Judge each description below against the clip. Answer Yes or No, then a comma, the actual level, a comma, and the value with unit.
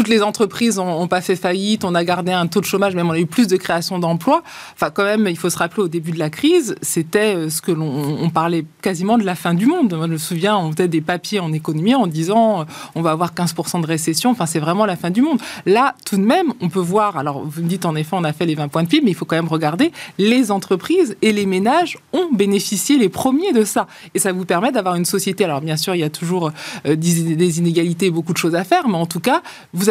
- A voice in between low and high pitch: Yes, medium, 180 Hz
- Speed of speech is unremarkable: No, fast, 275 wpm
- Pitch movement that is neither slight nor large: Yes, average, 3.9 semitones